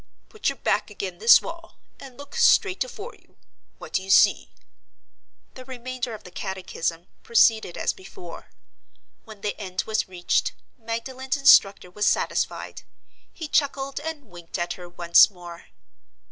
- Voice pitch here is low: No, high, 220 Hz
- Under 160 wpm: Yes, average, 145 wpm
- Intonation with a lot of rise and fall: Yes, wide, 6.9 semitones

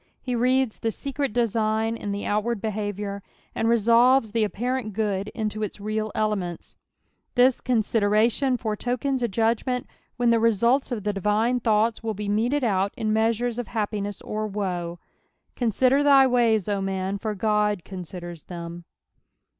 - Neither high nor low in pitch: No, high, 220 Hz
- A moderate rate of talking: Yes, average, 155 wpm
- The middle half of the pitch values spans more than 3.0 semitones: No, average, 2.7 semitones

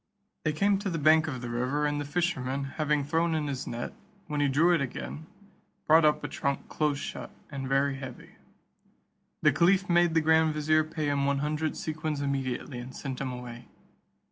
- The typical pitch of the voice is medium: Yes, medium, 150 Hz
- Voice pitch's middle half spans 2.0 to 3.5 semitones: Yes, narrow, 2.6 semitones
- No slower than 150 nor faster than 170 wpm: No, average, 195 wpm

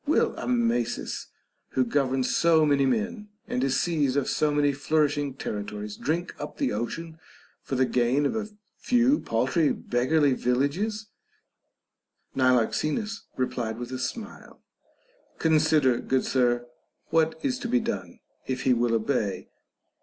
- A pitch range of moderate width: Yes, average, 4.7 semitones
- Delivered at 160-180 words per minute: No, average, 140 wpm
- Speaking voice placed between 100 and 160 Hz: Yes, medium, 140 Hz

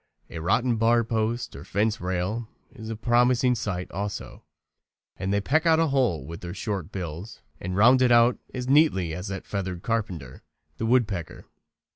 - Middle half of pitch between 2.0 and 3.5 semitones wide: No, average, 4.7 semitones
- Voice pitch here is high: No, low, 110 Hz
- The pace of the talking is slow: No, average, 175 wpm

